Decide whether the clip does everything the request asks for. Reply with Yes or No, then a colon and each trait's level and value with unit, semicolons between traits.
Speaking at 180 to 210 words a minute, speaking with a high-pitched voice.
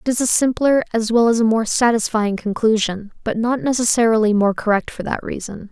Yes: average, 200 wpm; high, 225 Hz